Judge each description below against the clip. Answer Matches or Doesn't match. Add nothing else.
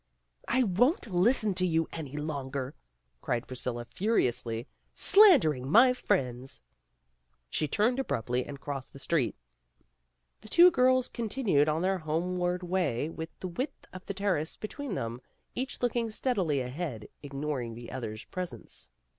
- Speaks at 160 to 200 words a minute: Doesn't match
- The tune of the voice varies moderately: Doesn't match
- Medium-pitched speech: Matches